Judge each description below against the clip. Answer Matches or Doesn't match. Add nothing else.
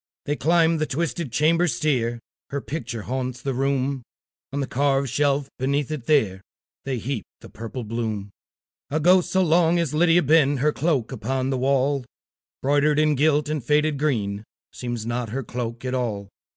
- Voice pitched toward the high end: Doesn't match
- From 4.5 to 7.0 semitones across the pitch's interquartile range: Doesn't match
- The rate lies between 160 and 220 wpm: Matches